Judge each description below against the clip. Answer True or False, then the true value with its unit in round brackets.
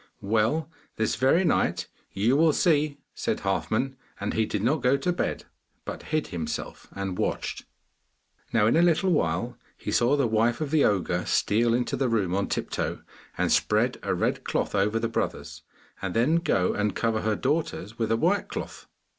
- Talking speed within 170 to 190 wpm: True (180 wpm)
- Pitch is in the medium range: False (115 Hz)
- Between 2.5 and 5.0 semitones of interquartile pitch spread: False (5.5 semitones)